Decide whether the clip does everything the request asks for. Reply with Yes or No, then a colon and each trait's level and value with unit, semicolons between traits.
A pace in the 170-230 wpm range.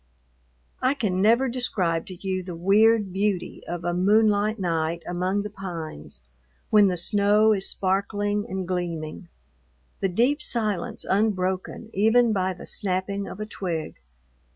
No: average, 140 wpm